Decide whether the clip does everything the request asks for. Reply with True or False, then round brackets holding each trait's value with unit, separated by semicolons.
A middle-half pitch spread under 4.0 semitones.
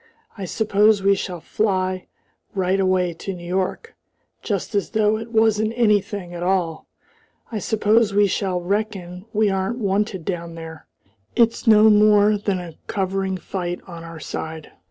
True (2.8 semitones)